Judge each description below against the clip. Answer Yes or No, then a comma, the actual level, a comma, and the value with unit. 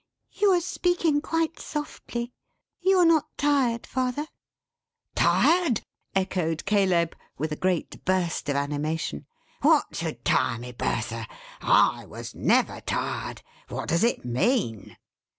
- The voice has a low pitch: No, high, 200 Hz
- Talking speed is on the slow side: Yes, slow, 125 wpm